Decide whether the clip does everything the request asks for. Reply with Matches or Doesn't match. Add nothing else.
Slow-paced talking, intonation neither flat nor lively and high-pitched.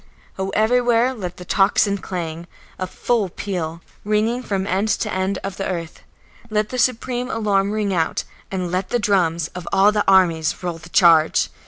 Doesn't match